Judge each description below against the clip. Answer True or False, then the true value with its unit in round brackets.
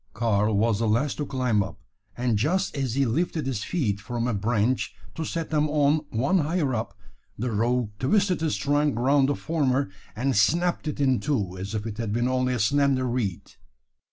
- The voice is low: True (130 Hz)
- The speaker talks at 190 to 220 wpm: True (195 wpm)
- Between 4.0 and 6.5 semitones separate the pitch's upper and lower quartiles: True (4.7 semitones)